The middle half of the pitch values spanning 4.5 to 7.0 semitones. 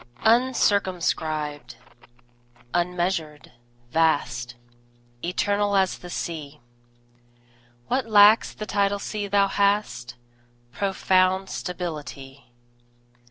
Yes: average, 4.8 semitones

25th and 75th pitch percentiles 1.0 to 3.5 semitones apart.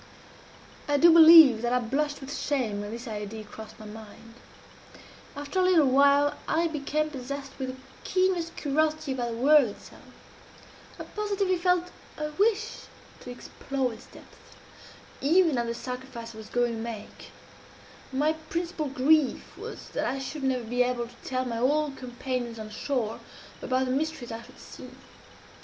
No: average, 4.3 semitones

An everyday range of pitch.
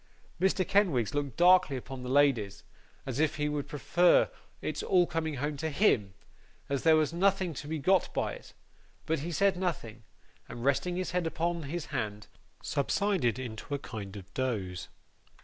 No: wide, 5.7 semitones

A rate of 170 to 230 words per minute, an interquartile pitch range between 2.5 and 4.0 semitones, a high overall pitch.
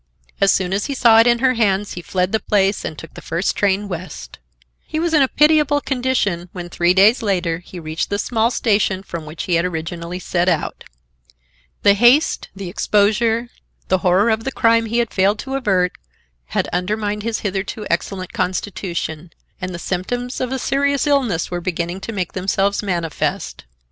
No: average, 185 wpm; average, 4.4 semitones; high, 200 Hz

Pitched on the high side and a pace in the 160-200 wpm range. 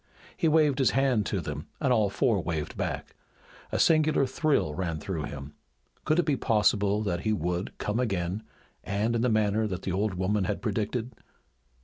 No: low, 105 Hz; average, 180 wpm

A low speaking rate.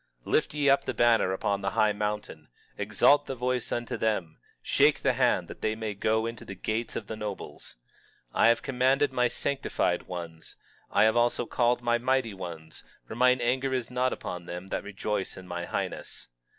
No: average, 195 wpm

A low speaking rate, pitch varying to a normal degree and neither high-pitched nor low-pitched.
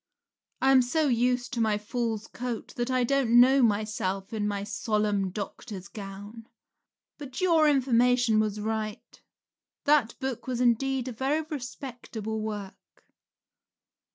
No: slow, 130 wpm; average, 3.5 semitones; high, 235 Hz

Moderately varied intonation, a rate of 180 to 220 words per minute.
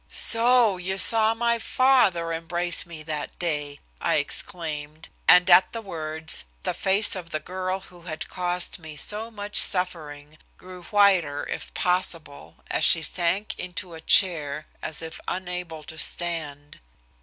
No: average, 3.4 semitones; average, 145 wpm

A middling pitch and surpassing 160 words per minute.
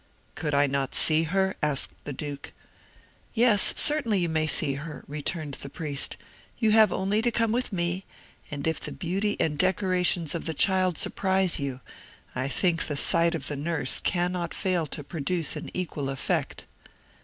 Yes: medium, 170 Hz; average, 170 wpm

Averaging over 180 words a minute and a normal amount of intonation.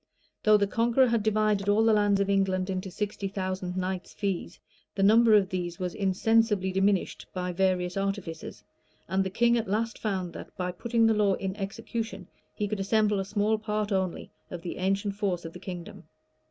No: average, 190 wpm; narrow, 2.3 semitones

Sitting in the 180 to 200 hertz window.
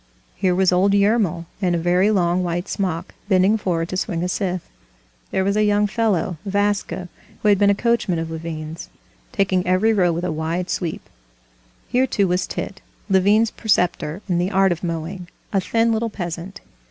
Yes: medium, 185 Hz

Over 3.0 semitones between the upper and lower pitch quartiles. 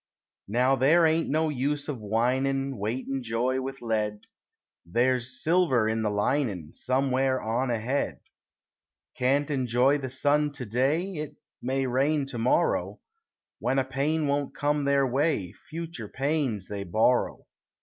Yes: average, 3.4 semitones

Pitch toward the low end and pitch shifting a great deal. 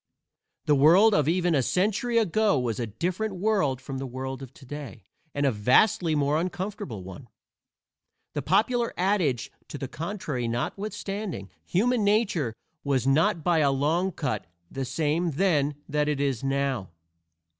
No: medium, 150 Hz; wide, 6.1 semitones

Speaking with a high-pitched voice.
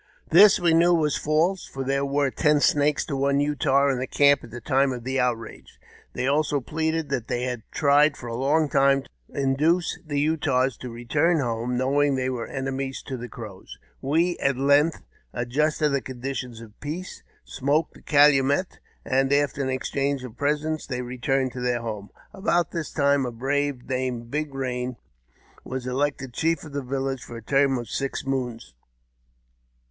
No: low, 135 Hz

